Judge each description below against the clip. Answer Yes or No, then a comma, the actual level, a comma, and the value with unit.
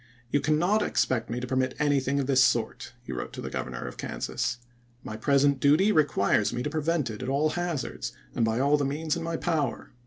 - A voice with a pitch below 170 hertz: Yes, medium, 140 Hz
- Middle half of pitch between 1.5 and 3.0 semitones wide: No, average, 3.7 semitones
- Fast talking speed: Yes, fast, 215 wpm